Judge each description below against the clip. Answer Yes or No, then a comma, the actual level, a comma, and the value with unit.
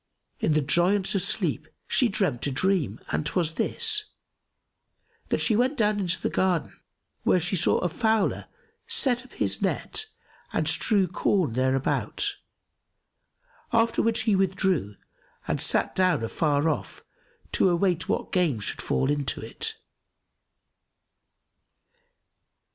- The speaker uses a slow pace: Yes, slow, 130 wpm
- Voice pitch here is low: No, medium, 185 Hz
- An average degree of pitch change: No, wide, 6.1 semitones